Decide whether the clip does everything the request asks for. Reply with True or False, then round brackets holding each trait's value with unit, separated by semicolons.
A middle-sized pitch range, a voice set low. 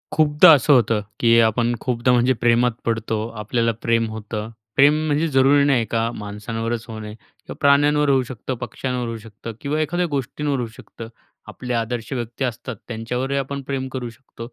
True (3.2 semitones; 120 Hz)